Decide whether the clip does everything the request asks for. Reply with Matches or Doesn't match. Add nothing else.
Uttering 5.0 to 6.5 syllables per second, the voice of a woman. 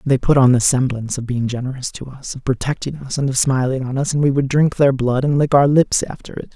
Doesn't match